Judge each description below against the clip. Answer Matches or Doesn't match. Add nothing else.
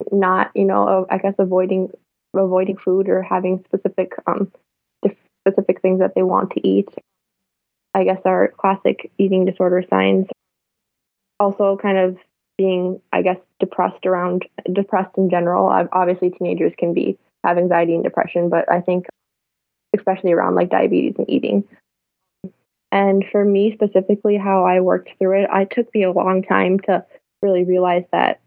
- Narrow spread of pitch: Matches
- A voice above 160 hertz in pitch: Matches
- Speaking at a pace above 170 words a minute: Doesn't match